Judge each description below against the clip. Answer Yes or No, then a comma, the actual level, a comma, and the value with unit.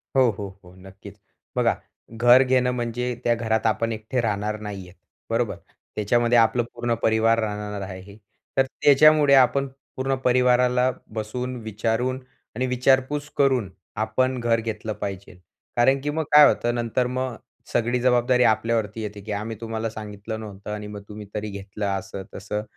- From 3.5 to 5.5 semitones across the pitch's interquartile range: No, average, 3.1 semitones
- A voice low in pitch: Yes, low, 115 Hz